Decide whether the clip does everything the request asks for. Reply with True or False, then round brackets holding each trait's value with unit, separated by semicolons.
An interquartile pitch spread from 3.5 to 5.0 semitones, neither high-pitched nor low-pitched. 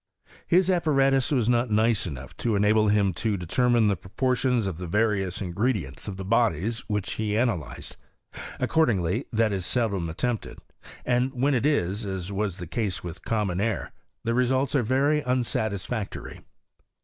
False (4.4 semitones; 110 Hz)